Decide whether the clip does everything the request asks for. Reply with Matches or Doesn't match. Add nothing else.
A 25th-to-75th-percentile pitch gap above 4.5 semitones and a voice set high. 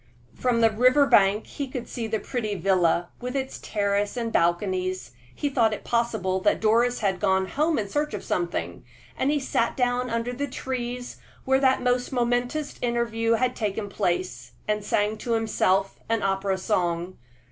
Doesn't match